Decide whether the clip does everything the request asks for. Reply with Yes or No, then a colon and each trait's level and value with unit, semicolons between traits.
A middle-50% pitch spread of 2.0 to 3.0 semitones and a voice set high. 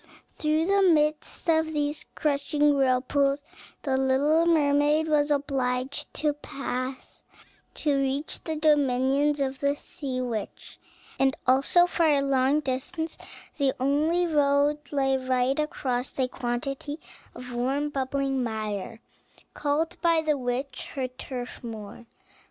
Yes: narrow, 2.6 semitones; very high, 280 Hz